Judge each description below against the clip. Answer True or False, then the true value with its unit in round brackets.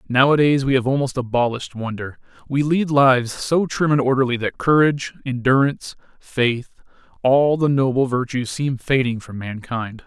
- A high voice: False (130 Hz)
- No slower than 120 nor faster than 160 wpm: True (150 wpm)